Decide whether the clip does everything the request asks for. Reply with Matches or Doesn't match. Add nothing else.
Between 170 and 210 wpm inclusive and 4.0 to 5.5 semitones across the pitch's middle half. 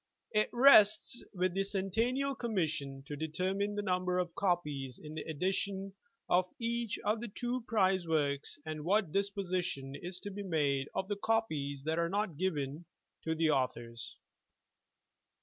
Doesn't match